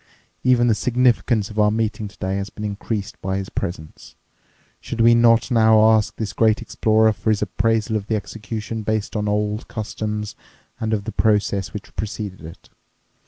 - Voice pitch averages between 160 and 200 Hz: No, low, 110 Hz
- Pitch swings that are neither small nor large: No, narrow, 1.4 semitones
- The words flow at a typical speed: Yes, average, 170 wpm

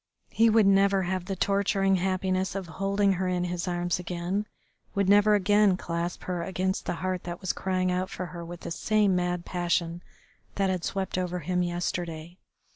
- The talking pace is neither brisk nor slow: Yes, average, 185 wpm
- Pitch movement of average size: No, narrow, 1.8 semitones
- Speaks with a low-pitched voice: No, medium, 185 Hz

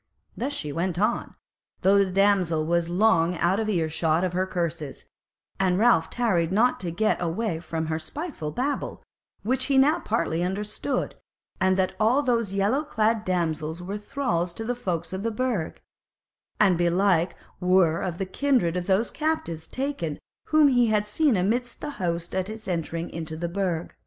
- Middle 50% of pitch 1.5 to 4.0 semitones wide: No, average, 5.2 semitones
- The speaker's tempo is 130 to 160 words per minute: No, average, 175 wpm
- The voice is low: No, high, 190 Hz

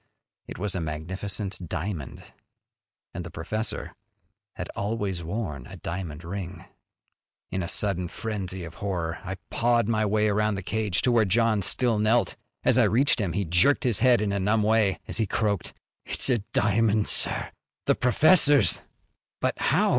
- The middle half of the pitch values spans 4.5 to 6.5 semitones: No, average, 3.7 semitones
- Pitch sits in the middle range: No, low, 100 Hz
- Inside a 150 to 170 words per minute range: Yes, average, 165 wpm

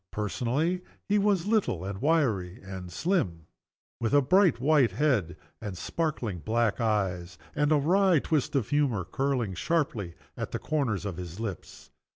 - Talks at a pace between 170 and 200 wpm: No, average, 155 wpm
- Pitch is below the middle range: Yes, low, 120 Hz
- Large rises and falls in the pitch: Yes, wide, 8.2 semitones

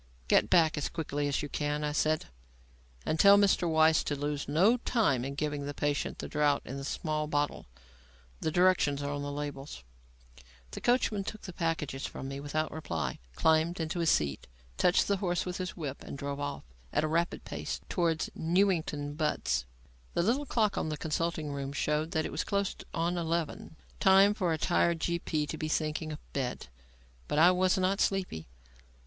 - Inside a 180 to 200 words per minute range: Yes, average, 190 wpm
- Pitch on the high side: No, medium, 155 Hz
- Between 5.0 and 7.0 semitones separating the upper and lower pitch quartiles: No, average, 3.4 semitones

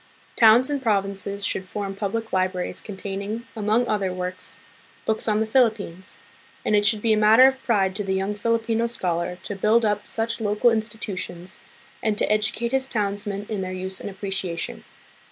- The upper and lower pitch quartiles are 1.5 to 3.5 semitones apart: Yes, narrow, 2.6 semitones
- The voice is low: No, high, 210 Hz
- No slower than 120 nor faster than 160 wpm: No, average, 170 wpm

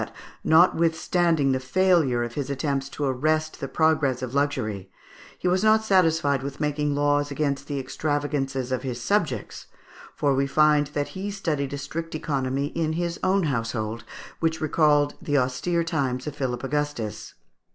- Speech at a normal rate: Yes, average, 160 wpm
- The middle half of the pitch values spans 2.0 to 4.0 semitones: Yes, average, 3.1 semitones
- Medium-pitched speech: Yes, medium, 145 Hz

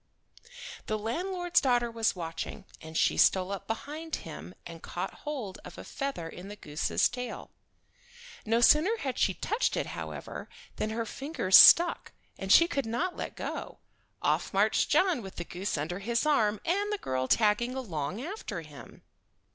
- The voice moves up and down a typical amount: No, wide, 8.2 semitones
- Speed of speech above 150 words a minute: Yes, average, 165 wpm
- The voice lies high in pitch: Yes, high, 225 Hz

